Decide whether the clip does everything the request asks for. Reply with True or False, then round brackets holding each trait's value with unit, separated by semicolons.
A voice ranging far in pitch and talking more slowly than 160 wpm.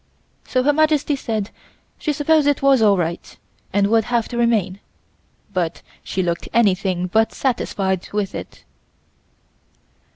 True (5.9 semitones; 135 wpm)